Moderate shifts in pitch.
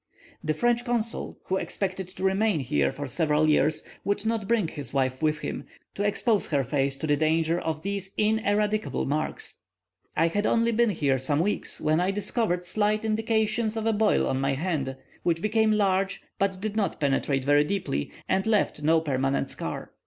No: wide, 6.1 semitones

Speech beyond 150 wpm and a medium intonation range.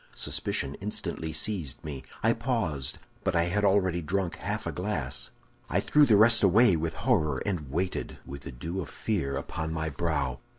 No: average, 175 wpm; wide, 5.7 semitones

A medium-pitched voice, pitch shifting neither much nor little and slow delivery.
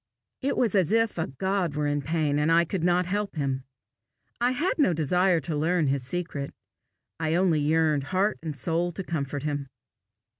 No: medium, 165 Hz; average, 4.1 semitones; average, 185 wpm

